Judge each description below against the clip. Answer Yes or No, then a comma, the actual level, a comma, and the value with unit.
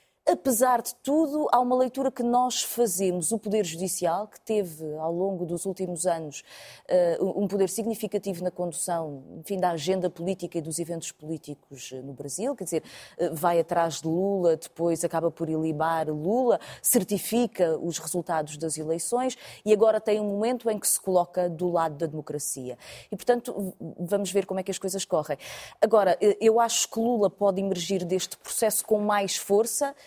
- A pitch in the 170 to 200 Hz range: Yes, high, 190 Hz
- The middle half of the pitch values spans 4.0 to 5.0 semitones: Yes, average, 4.4 semitones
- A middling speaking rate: Yes, average, 170 wpm